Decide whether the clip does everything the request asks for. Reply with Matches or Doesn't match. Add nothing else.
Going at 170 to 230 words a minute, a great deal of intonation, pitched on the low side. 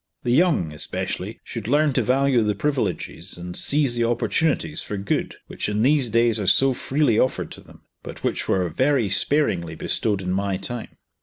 Matches